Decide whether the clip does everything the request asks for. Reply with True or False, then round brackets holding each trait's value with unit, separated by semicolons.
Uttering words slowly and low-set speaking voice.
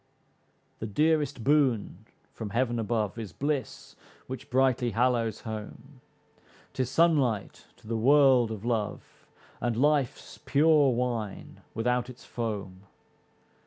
True (115 wpm; 120 Hz)